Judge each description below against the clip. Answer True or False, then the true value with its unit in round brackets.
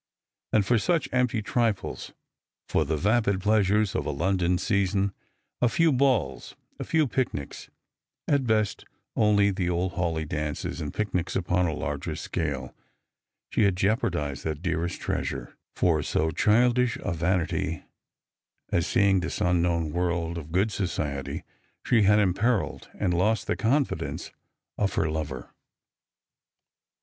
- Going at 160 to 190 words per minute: False (140 wpm)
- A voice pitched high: False (95 Hz)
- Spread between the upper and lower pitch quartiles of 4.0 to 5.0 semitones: True (4.7 semitones)